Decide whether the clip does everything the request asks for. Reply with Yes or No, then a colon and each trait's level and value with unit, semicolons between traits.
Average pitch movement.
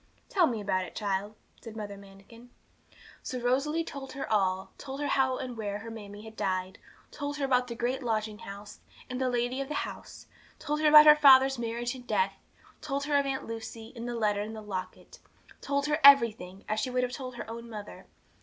Yes: average, 4.4 semitones